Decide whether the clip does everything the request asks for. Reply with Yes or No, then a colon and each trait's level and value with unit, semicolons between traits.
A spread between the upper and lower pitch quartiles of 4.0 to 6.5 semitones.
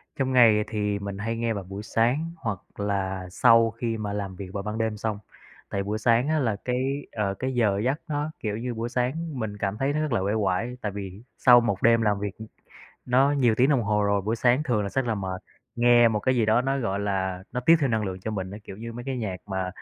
No: average, 3.5 semitones